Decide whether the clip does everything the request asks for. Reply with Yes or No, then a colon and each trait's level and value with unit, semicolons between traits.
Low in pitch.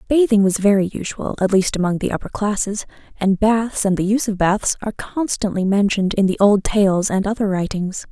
No: high, 200 Hz